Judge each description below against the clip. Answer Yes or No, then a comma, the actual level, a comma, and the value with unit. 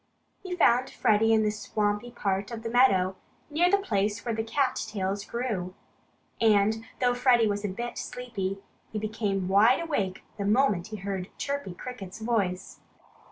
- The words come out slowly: No, average, 160 wpm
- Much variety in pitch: No, average, 3.6 semitones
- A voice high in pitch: Yes, high, 215 Hz